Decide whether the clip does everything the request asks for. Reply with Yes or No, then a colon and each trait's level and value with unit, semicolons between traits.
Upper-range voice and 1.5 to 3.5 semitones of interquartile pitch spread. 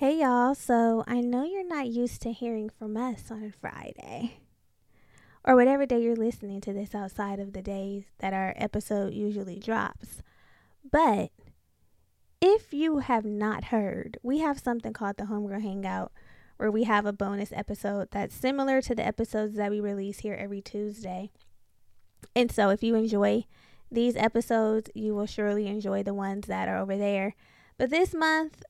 Yes: high, 215 Hz; average, 3.2 semitones